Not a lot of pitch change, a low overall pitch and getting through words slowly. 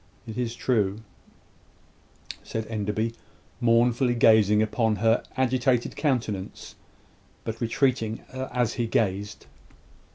Yes: narrow, 2.3 semitones; low, 115 Hz; slow, 95 wpm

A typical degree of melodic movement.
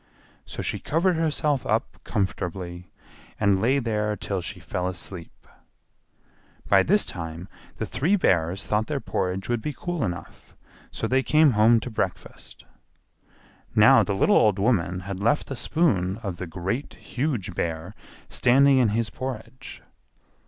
No: wide, 6.4 semitones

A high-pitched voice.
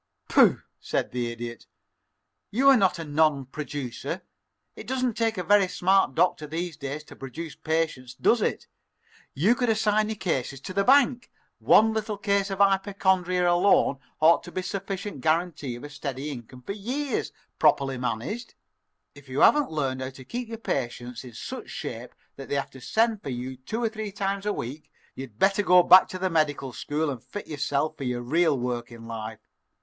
No: medium, 160 Hz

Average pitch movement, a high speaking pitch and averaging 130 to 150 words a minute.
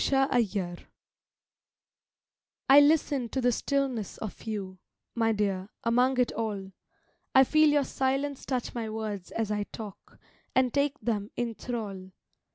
Yes: average, 4.4 semitones; high, 230 Hz; slow, 135 wpm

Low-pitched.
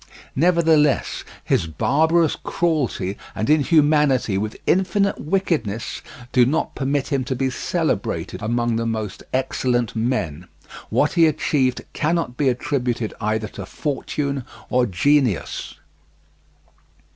Yes: low, 130 Hz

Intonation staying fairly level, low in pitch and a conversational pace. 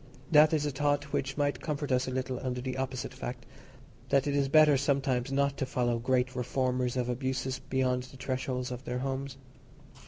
Yes: narrow, 1.7 semitones; low, 130 Hz; average, 185 wpm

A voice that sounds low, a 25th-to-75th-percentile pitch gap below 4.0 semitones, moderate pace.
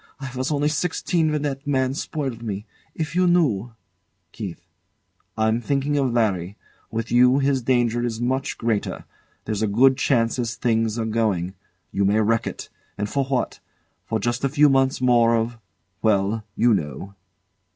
Yes: low, 120 Hz; average, 3.5 semitones; average, 160 wpm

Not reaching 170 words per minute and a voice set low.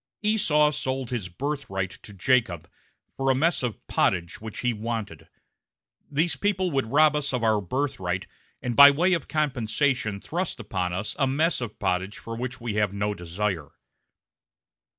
Yes: average, 160 wpm; low, 125 Hz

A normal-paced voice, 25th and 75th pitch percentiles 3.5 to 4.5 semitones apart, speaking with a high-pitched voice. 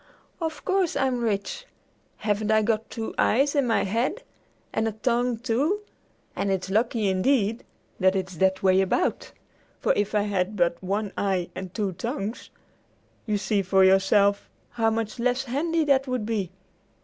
Yes: average, 160 wpm; average, 4.2 semitones; high, 215 Hz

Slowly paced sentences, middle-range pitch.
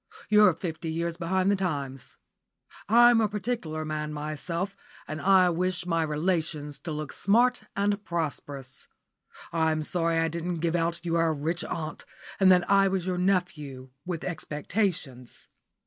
No: average, 150 wpm; medium, 170 Hz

